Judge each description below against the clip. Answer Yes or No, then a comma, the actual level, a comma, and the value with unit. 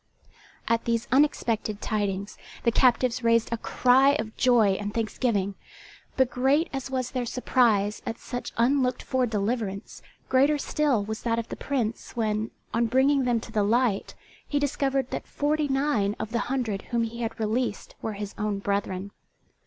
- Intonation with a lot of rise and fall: No, average, 3.5 semitones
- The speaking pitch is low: No, high, 235 Hz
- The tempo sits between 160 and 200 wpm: Yes, average, 165 wpm